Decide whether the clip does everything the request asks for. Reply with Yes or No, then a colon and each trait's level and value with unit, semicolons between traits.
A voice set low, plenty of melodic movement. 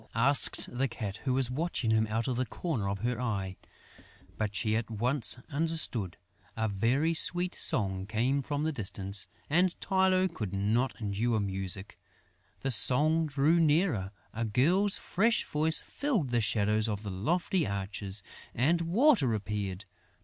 Yes: low, 120 Hz; wide, 7.2 semitones